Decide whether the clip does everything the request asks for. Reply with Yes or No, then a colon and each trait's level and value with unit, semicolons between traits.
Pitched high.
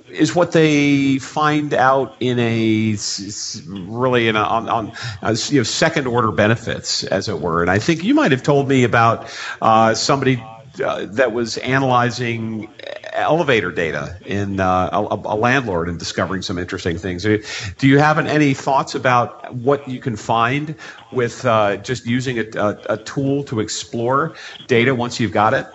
No: low, 120 Hz